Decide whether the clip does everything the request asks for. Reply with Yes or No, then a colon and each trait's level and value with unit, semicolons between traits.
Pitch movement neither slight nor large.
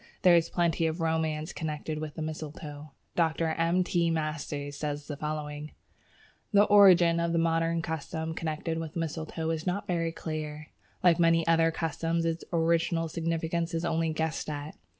No: narrow, 1.3 semitones